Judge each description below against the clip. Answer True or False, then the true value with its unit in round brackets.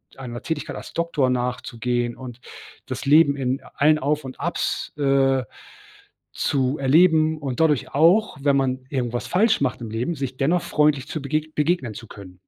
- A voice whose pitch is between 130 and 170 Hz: True (140 Hz)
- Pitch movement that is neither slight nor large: True (3.5 semitones)